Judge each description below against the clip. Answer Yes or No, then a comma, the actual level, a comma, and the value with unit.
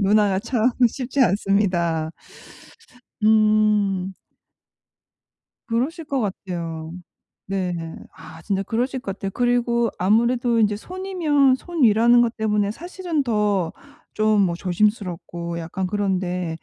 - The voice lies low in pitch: No, high, 210 Hz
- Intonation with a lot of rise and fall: No, average, 4.3 semitones